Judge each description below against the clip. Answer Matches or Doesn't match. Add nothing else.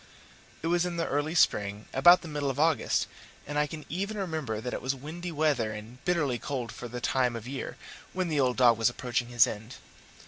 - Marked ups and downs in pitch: Doesn't match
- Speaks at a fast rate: Matches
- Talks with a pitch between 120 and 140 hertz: Matches